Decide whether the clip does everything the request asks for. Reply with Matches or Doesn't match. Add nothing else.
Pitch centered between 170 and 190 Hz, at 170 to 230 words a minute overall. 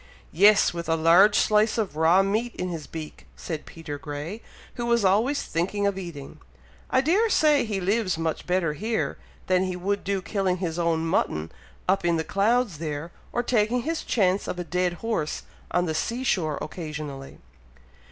Matches